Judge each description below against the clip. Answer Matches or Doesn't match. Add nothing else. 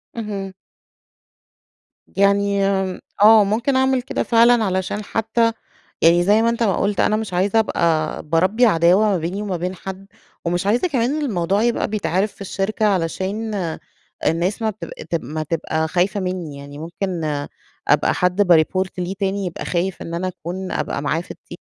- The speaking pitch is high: Matches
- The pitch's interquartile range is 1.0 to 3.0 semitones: Doesn't match